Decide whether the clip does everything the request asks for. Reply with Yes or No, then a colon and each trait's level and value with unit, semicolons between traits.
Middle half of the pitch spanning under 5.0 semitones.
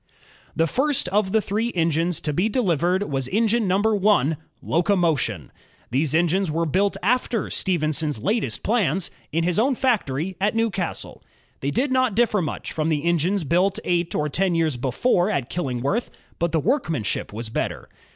No: average, 5.3 semitones